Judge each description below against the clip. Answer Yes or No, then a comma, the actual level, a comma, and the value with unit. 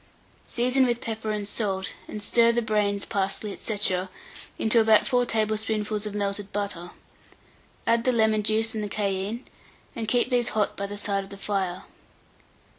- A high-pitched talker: Yes, high, 215 Hz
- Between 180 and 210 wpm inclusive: No, average, 160 wpm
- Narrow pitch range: Yes, narrow, 2.1 semitones